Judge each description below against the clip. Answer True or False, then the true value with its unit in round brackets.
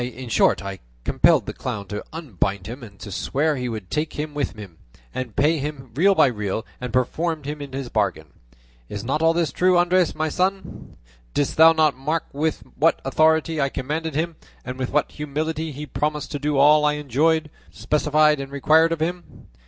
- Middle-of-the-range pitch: True (150 Hz)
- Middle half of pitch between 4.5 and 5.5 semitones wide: False (3.8 semitones)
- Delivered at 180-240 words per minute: True (190 wpm)